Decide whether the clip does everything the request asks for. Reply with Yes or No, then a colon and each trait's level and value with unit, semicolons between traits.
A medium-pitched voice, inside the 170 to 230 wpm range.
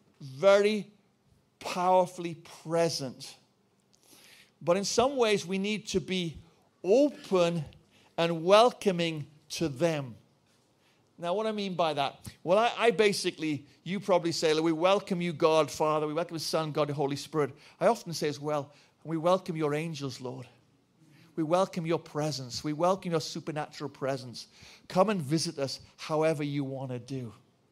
No: medium, 160 Hz; average, 150 wpm